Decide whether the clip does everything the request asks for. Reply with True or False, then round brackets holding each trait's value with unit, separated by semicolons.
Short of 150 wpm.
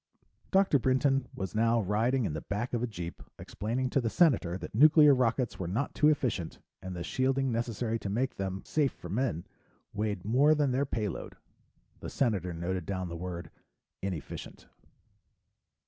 False (165 wpm)